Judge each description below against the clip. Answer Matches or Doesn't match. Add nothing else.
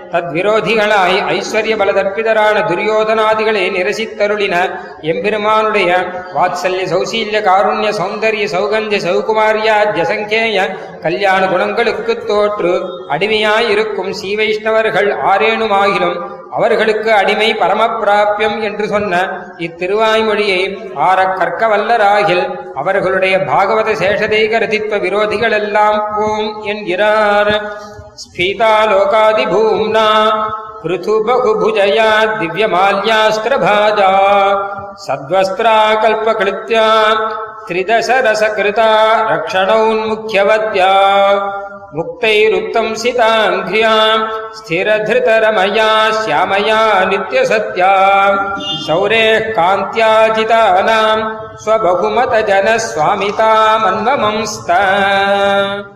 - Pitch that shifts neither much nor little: Doesn't match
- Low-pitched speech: Doesn't match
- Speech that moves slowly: Matches